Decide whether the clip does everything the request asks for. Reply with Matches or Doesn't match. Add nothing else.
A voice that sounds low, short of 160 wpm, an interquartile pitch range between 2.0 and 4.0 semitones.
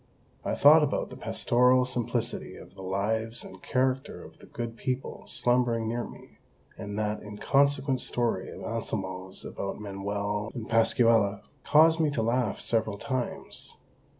Matches